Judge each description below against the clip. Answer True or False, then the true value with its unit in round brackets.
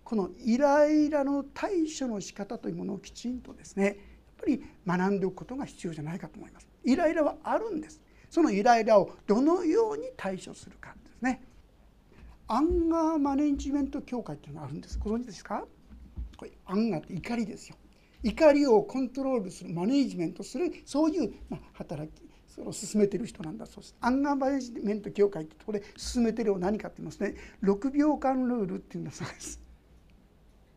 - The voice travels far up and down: True (6.3 semitones)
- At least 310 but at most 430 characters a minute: True (405 characters per minute)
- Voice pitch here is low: False (240 Hz)